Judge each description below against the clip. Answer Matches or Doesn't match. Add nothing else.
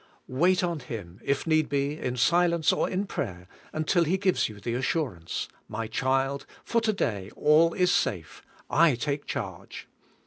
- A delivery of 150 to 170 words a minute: Matches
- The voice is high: Doesn't match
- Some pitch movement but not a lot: Doesn't match